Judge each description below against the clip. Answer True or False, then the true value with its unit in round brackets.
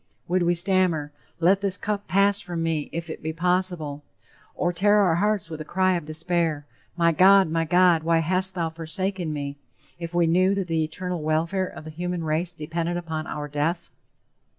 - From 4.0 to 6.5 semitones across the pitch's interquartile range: False (2.6 semitones)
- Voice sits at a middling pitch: True (170 Hz)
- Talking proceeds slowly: False (190 wpm)